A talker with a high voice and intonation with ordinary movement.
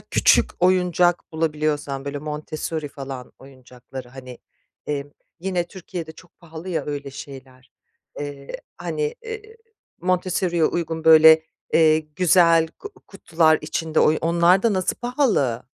No: medium, 160 Hz; average, 3.5 semitones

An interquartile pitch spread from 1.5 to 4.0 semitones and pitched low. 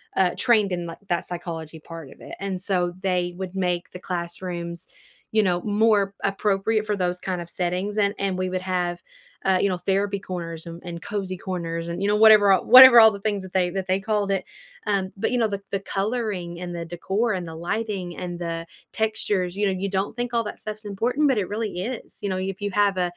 No: average, 2.7 semitones; high, 190 Hz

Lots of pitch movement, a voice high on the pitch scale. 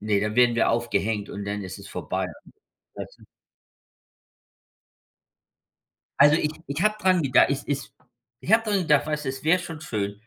No: wide, 7.1 semitones; low, 135 Hz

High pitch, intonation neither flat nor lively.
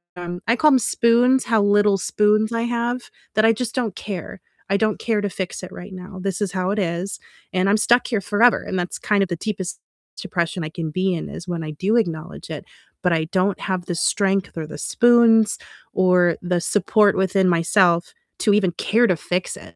Yes: high, 195 Hz; average, 3.4 semitones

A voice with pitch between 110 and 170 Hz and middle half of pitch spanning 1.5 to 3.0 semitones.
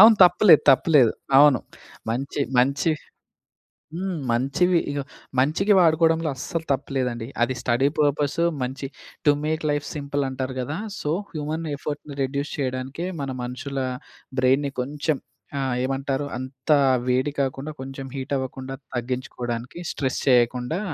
Yes: medium, 140 Hz; average, 2.7 semitones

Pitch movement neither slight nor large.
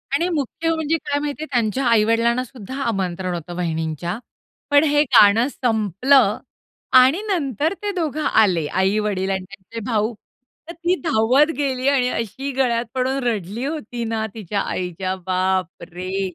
No: wide, 6.6 semitones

